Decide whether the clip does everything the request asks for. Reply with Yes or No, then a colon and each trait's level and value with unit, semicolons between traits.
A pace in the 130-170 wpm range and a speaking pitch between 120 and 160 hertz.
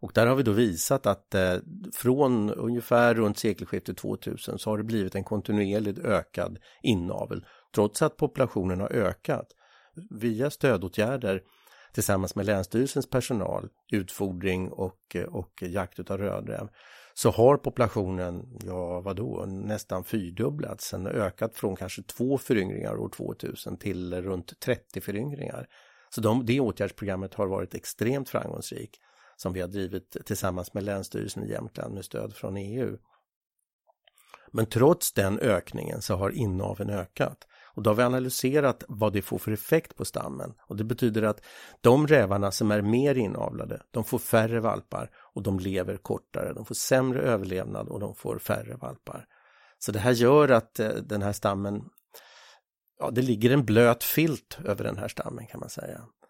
No: average, 155 wpm; low, 105 Hz